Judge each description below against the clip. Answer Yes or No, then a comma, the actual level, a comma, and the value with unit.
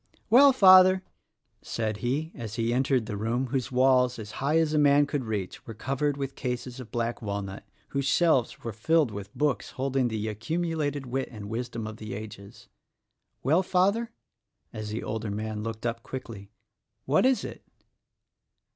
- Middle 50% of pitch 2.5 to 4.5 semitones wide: No, average, 4.9 semitones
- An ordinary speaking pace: Yes, average, 170 wpm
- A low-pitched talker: Yes, low, 125 Hz